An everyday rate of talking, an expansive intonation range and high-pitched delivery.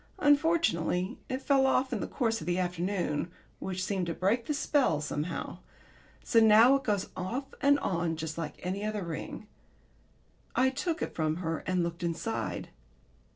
Yes: average, 165 wpm; wide, 7.2 semitones; high, 195 Hz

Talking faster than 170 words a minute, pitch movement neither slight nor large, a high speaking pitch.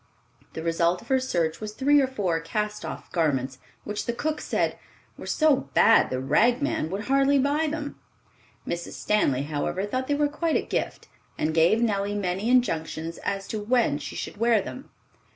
No: average, 185 wpm; wide, 7.8 semitones; high, 210 Hz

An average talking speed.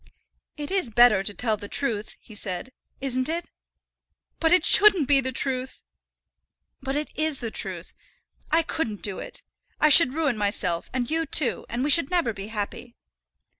Yes: average, 170 wpm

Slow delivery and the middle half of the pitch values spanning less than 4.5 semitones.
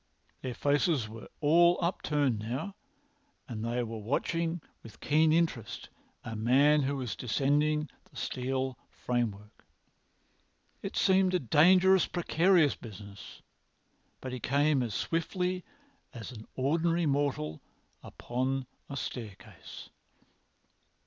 No: slow, 110 wpm; wide, 5.6 semitones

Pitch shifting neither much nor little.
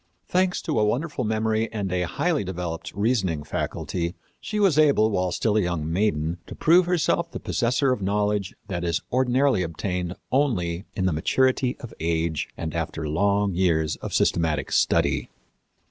No: wide, 6.8 semitones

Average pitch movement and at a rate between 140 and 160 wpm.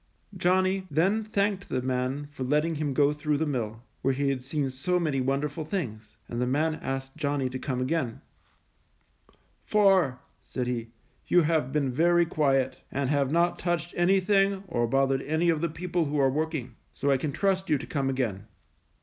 No: average, 4.5 semitones; average, 185 wpm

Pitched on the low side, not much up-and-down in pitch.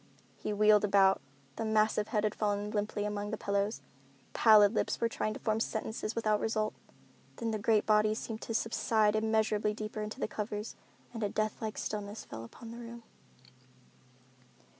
No: high, 215 Hz; narrow, 1.0 semitones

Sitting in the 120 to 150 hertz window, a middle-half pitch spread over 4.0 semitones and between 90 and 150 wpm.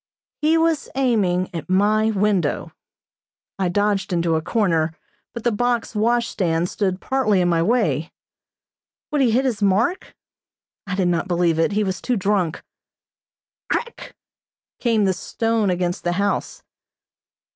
No: high, 200 Hz; average, 4.6 semitones; average, 140 wpm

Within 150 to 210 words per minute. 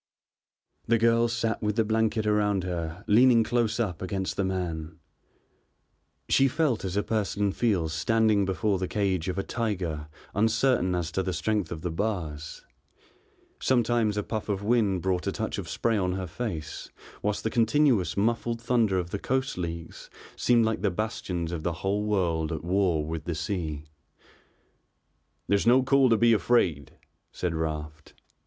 Yes: average, 165 wpm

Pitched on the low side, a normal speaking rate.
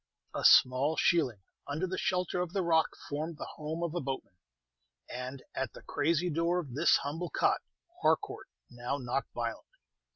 No: medium, 155 Hz; average, 165 wpm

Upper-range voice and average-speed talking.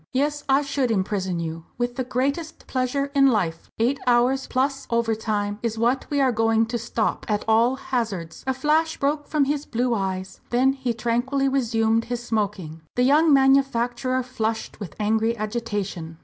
Yes: high, 240 Hz; average, 165 wpm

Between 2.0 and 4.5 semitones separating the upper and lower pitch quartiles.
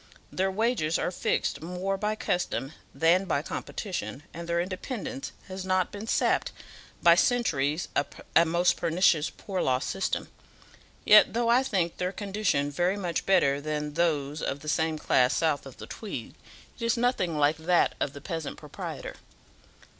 Yes: average, 4.2 semitones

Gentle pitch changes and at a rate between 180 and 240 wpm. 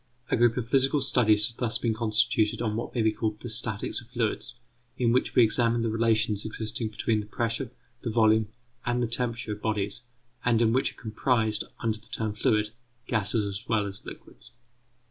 Yes: narrow, 1.8 semitones; average, 195 wpm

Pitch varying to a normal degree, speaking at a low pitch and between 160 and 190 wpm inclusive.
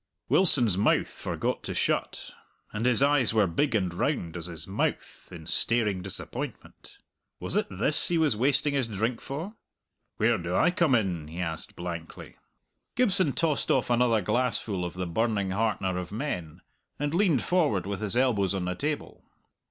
No: wide, 7.2 semitones; low, 110 Hz; average, 165 wpm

